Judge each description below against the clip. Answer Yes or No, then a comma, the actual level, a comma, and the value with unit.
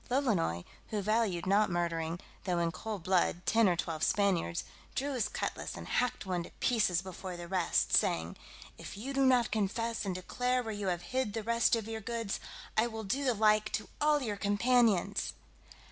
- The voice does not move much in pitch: No, average, 4.5 semitones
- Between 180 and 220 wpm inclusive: Yes, average, 190 wpm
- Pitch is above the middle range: Yes, high, 210 Hz